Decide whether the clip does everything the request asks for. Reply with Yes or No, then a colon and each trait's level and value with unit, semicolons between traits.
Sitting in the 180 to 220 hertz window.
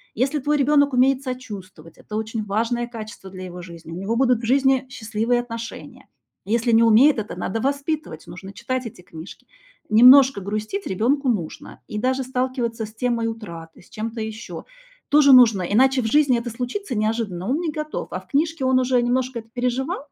No: high, 235 Hz